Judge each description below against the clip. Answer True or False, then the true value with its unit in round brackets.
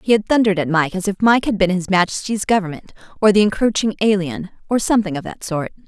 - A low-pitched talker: False (195 Hz)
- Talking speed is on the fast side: True (225 wpm)